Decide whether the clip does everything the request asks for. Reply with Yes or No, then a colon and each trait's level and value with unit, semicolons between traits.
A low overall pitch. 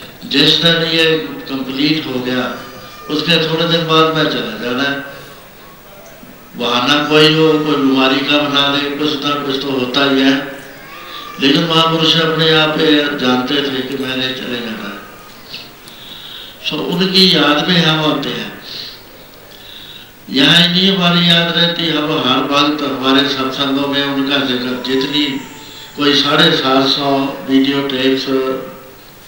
No: medium, 145 Hz